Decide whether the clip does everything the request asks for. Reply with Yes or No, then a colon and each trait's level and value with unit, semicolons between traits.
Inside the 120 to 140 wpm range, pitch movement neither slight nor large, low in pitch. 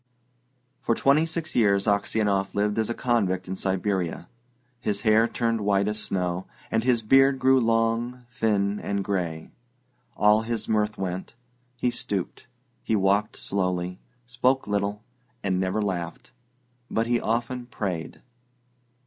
Yes: slow, 135 wpm; average, 3.4 semitones; low, 105 Hz